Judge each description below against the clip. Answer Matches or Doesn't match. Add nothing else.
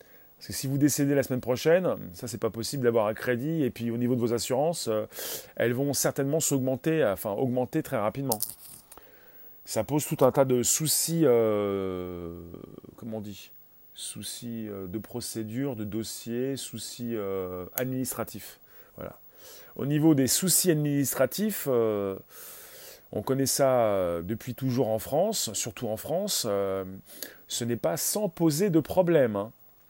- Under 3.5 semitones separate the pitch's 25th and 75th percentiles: Doesn't match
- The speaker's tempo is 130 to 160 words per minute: Matches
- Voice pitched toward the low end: Matches